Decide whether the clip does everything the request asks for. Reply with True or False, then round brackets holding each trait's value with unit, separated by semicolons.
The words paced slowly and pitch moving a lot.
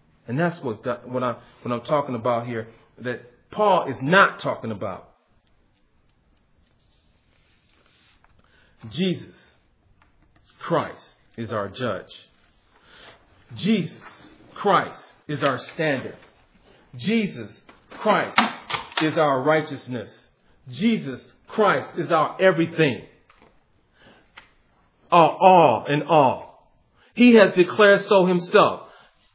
True (95 wpm; 7.0 semitones)